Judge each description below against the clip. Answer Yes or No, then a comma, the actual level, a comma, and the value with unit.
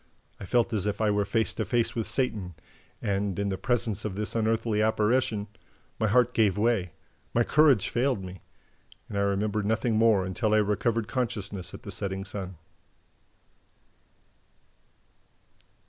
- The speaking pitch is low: Yes, low, 105 Hz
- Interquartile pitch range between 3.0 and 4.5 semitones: No, narrow, 2.5 semitones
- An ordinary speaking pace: Yes, average, 150 wpm